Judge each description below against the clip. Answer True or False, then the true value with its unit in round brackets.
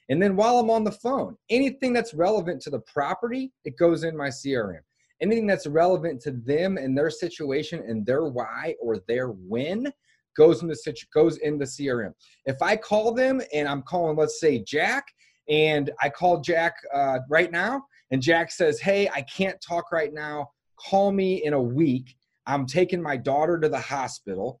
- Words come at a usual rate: True (190 wpm)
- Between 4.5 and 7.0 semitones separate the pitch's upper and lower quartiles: True (5.5 semitones)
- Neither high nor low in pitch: True (160 Hz)